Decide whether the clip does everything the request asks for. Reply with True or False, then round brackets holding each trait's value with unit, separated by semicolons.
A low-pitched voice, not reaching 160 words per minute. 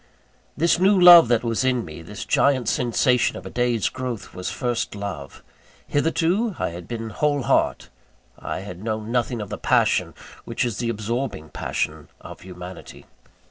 False (115 Hz; 165 wpm)